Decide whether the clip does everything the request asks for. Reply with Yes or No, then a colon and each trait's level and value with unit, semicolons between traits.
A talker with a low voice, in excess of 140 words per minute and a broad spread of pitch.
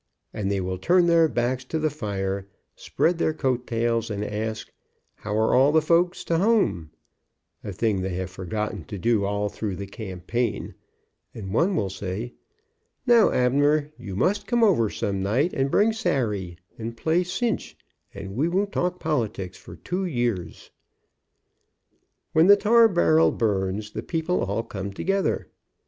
Yes: low, 120 Hz; average, 160 wpm; wide, 8.9 semitones